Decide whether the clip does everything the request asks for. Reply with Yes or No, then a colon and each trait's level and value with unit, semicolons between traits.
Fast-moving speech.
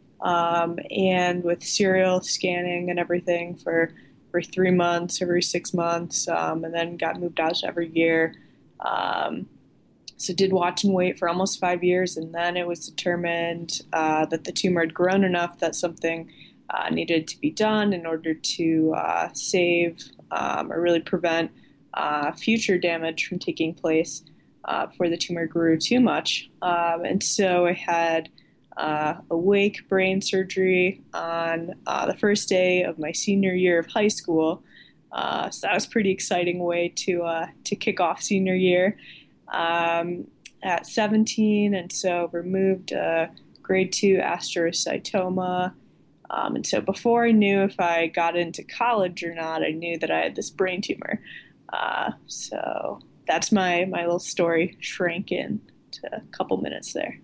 No: average, 160 wpm